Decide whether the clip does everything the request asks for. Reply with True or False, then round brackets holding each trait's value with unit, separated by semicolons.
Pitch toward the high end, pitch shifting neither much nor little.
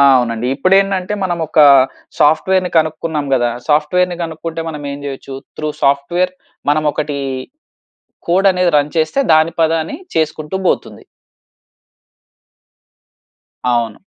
False (155 Hz; 3.4 semitones)